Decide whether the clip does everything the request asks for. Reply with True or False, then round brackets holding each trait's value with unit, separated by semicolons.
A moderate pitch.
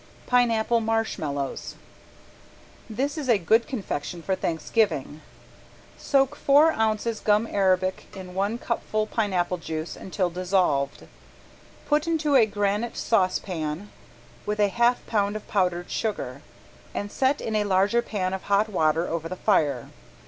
False (205 Hz)